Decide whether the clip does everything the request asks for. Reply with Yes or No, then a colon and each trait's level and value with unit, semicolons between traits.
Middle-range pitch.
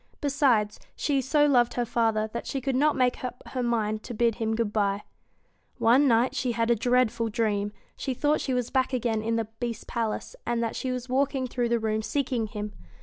No: high, 235 Hz